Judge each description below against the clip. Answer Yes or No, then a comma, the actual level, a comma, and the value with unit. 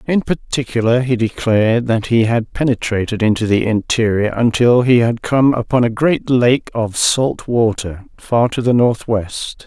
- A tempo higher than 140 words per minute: Yes, average, 160 wpm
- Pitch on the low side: Yes, low, 115 Hz